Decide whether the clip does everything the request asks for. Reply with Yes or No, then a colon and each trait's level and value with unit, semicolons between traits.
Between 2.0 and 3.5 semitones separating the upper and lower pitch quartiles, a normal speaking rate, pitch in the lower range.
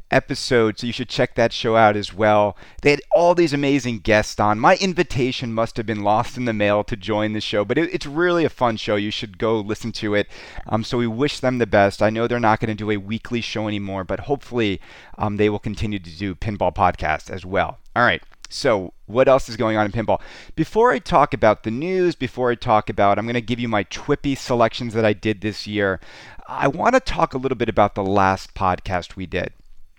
No: average, 3.1 semitones; fast, 240 wpm; low, 110 Hz